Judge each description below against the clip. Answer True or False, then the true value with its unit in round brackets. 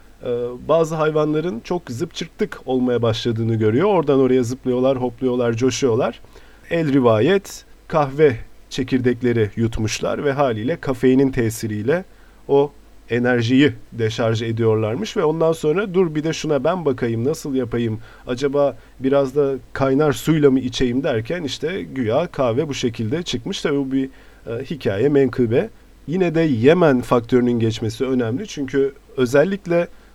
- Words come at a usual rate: True (125 wpm)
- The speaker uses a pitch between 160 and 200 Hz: False (135 Hz)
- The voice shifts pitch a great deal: False (3.8 semitones)